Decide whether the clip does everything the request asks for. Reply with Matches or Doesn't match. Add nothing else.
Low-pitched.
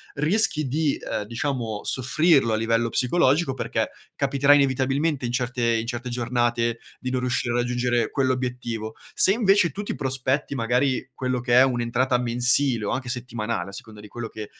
Matches